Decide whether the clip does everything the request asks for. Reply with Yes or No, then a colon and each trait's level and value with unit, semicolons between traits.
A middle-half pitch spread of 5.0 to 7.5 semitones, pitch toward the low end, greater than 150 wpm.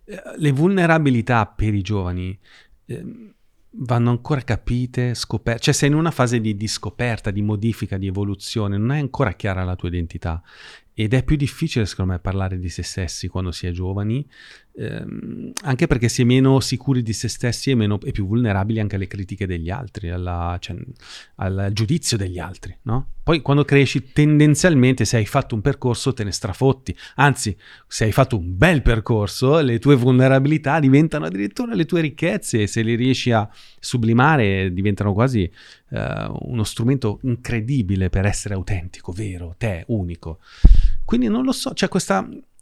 Yes: wide, 5.4 semitones; low, 115 Hz; fast, 170 wpm